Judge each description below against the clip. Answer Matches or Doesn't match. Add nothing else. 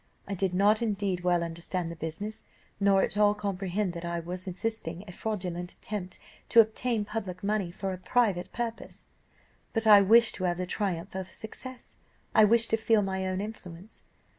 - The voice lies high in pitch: Matches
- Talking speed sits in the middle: Matches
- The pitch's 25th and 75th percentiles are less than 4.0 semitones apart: Matches